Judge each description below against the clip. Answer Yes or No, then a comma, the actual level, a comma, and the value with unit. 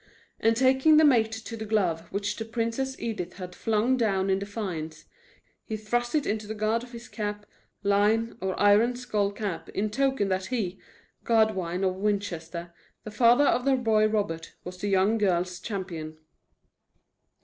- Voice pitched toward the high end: Yes, high, 210 Hz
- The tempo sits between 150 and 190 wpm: Yes, average, 165 wpm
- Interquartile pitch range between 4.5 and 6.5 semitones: No, average, 3.4 semitones